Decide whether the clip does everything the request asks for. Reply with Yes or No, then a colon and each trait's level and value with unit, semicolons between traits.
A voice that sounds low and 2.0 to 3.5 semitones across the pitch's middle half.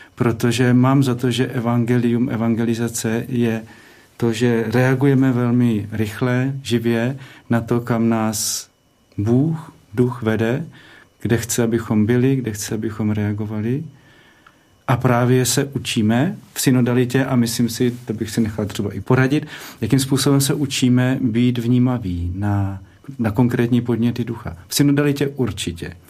Yes: low, 120 Hz; narrow, 2.4 semitones